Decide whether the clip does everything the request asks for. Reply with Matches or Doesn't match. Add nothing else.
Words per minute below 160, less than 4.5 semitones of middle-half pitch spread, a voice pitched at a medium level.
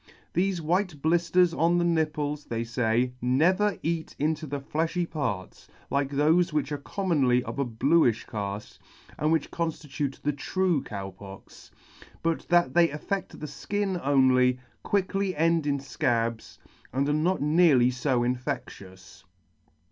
Doesn't match